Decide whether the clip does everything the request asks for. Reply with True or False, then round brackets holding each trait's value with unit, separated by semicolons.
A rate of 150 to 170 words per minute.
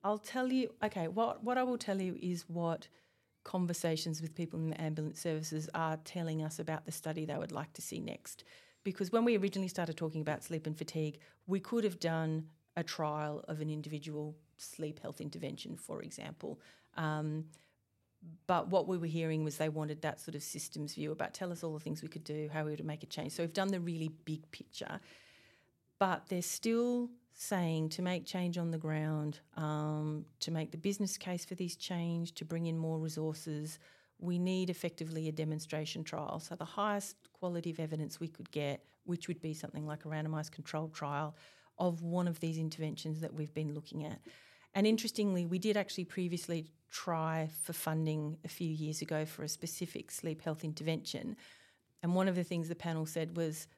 False (195 wpm)